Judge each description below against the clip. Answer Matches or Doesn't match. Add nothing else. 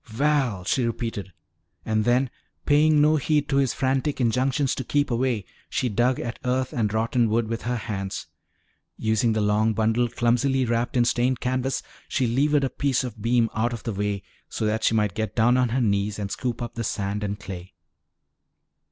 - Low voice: Matches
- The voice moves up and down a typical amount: Matches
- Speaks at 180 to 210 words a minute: Matches